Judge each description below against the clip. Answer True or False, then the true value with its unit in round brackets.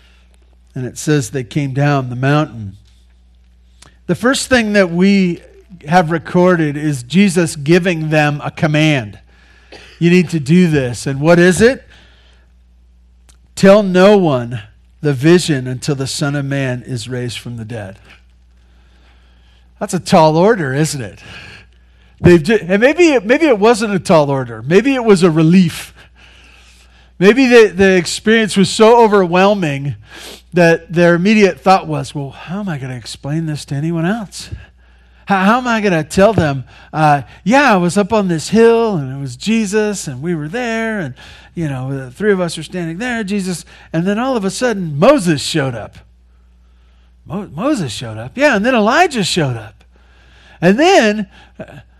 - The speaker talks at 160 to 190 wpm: True (170 wpm)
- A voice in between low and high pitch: True (155 Hz)